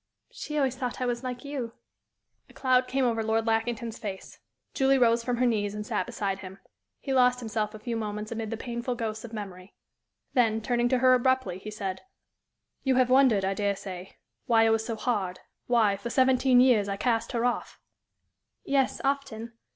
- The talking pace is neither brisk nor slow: Yes, average, 190 wpm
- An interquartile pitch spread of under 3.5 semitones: Yes, average, 3.0 semitones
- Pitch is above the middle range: Yes, high, 230 Hz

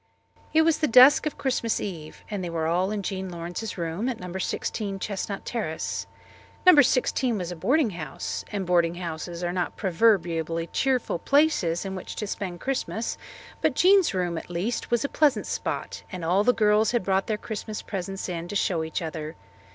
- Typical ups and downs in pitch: Yes, average, 5.0 semitones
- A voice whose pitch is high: Yes, high, 195 Hz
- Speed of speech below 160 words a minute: No, average, 190 wpm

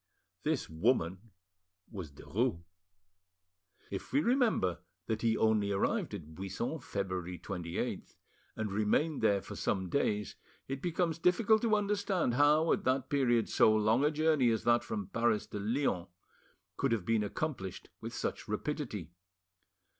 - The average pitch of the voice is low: Yes, low, 115 Hz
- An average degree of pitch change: No, wide, 7.0 semitones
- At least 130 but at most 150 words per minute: Yes, average, 140 wpm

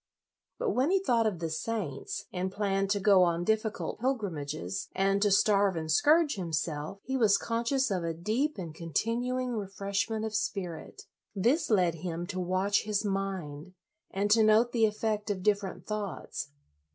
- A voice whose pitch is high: Yes, high, 200 Hz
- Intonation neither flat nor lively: Yes, average, 3.7 semitones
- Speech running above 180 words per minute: No, average, 175 wpm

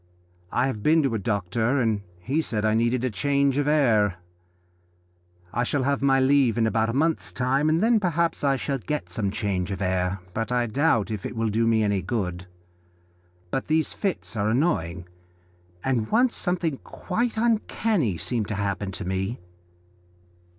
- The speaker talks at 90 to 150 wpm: No, average, 170 wpm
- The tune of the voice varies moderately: No, wide, 5.7 semitones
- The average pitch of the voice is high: No, low, 120 Hz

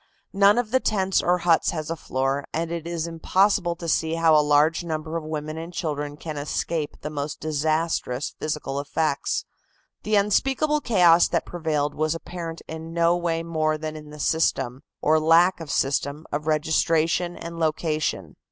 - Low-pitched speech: No, medium, 160 Hz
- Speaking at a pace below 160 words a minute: No, average, 170 wpm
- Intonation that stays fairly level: Yes, narrow, 2.0 semitones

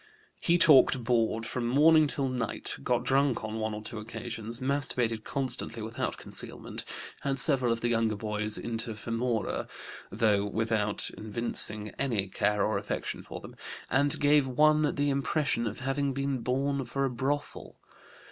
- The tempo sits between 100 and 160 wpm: Yes, average, 155 wpm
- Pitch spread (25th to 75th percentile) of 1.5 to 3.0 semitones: No, average, 3.7 semitones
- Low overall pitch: Yes, low, 120 Hz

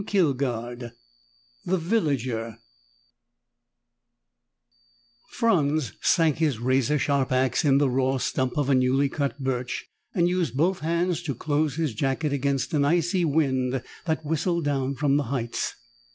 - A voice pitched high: No, medium, 140 Hz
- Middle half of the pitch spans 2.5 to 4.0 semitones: Yes, average, 3.6 semitones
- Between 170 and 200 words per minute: No, slow, 135 wpm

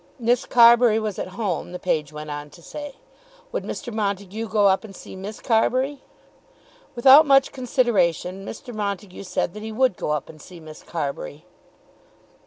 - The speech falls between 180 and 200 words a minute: No, average, 170 wpm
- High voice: Yes, high, 205 Hz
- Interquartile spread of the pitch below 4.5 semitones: No, average, 5.1 semitones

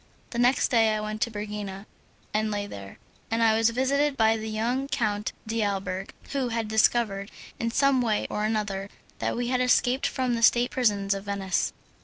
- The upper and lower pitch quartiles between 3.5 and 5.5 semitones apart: No, average, 2.8 semitones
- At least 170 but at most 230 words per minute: Yes, average, 180 wpm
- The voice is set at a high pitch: Yes, high, 220 Hz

